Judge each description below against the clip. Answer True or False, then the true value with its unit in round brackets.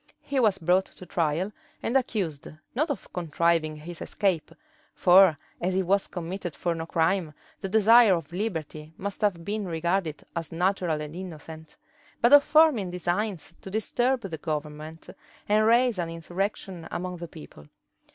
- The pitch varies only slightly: False (3.8 semitones)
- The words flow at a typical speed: True (155 wpm)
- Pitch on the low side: False (180 Hz)